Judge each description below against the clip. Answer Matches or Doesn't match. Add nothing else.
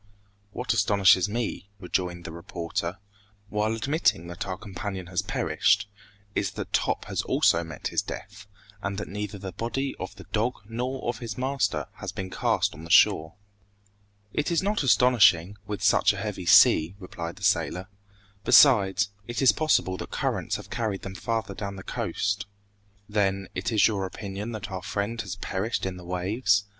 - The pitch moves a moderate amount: Matches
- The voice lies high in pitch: Doesn't match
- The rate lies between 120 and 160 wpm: Doesn't match